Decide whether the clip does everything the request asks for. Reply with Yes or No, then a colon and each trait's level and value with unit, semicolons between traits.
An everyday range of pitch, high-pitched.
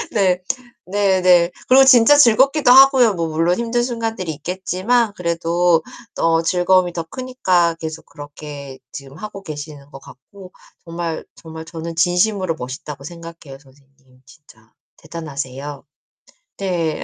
No: average, 4.8 semitones; medium, 170 Hz